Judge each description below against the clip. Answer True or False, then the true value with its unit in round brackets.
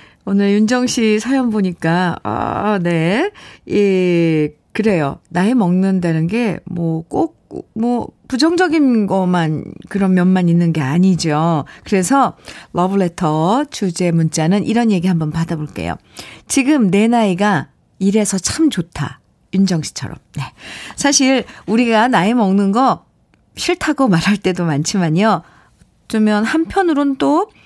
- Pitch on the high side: True (200 Hz)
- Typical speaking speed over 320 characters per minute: False (245 characters per minute)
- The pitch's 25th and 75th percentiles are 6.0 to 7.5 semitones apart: False (5.5 semitones)